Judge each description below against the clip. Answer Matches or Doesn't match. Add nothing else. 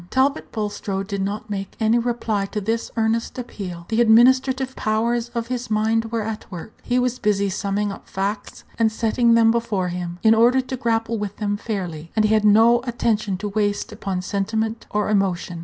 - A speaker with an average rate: Matches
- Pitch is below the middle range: Doesn't match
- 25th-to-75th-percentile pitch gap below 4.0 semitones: Matches